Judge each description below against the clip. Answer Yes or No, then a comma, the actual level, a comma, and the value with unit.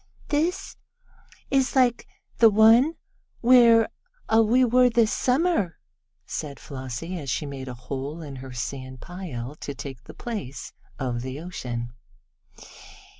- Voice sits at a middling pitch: Yes, medium, 165 Hz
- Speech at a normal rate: No, slow, 125 wpm